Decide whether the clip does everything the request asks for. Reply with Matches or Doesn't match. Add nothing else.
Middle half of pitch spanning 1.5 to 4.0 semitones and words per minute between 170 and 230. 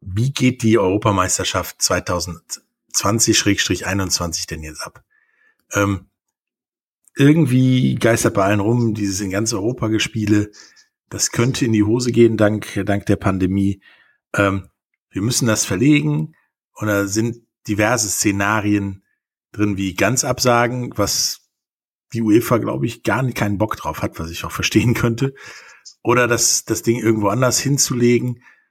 Doesn't match